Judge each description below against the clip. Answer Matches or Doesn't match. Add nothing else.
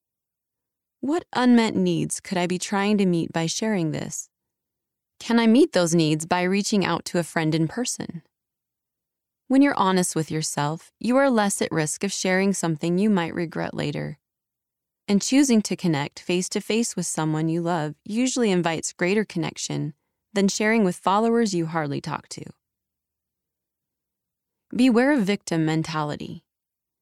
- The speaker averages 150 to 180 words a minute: Matches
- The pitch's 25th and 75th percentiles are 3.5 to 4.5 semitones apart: Doesn't match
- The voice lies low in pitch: Doesn't match